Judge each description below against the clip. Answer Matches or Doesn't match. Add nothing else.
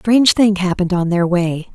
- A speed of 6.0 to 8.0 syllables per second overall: Matches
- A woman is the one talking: Matches